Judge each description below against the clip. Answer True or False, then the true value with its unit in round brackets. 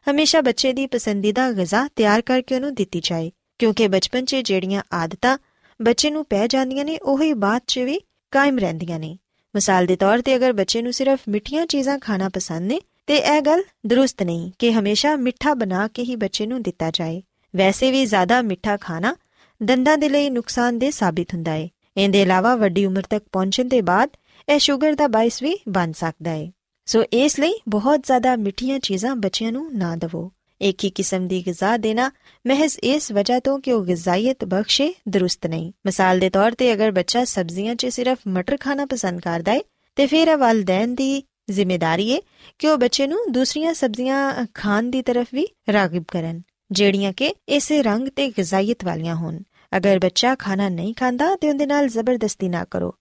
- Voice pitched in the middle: False (230 Hz)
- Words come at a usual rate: False (180 wpm)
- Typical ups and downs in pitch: False (5.8 semitones)